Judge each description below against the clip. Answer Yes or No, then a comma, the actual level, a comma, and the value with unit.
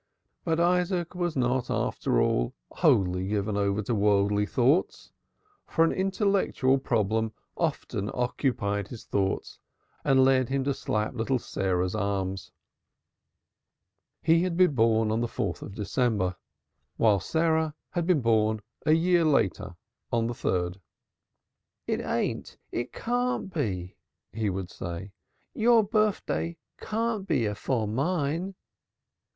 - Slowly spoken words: Yes, slow, 125 wpm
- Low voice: Yes, low, 120 Hz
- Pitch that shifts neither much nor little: No, wide, 8.4 semitones